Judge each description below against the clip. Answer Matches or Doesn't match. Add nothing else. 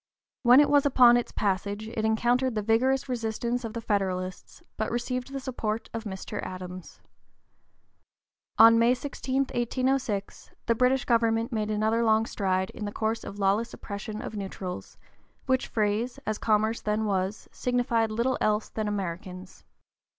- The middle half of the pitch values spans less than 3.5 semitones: Matches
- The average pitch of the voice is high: Matches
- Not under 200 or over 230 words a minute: Doesn't match